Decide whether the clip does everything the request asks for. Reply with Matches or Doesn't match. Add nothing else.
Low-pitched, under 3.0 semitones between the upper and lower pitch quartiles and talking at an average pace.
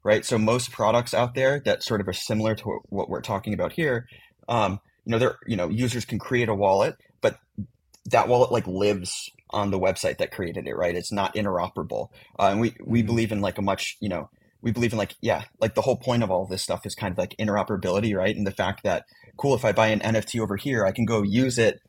Doesn't match